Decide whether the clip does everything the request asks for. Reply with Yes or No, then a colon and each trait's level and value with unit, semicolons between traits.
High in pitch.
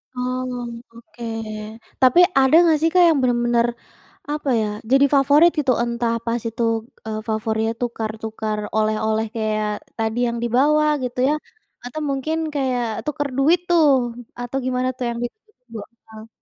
Yes: high, 245 Hz